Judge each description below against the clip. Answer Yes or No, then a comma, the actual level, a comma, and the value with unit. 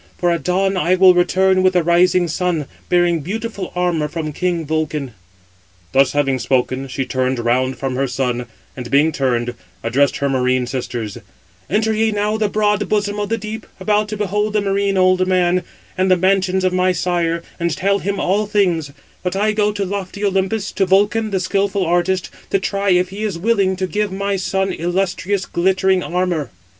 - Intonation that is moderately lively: Yes, average, 3.8 semitones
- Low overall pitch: No, medium, 185 Hz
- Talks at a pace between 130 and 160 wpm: No, average, 185 wpm